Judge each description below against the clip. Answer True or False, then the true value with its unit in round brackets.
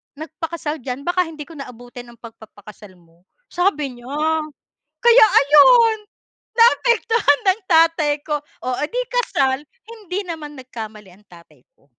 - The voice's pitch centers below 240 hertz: False (295 Hz)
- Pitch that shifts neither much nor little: False (7.0 semitones)